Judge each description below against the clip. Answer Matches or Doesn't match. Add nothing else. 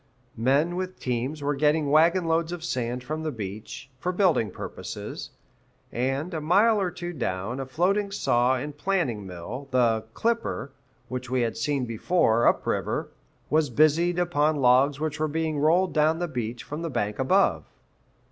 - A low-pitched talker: Doesn't match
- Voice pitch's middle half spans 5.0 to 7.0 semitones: Matches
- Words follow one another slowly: Doesn't match